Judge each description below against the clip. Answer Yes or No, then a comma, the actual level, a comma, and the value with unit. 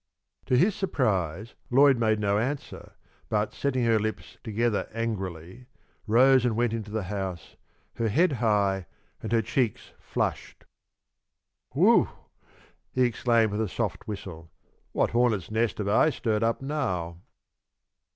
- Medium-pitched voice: No, low, 110 Hz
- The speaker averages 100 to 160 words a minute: Yes, slow, 135 wpm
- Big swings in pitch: No, average, 3.4 semitones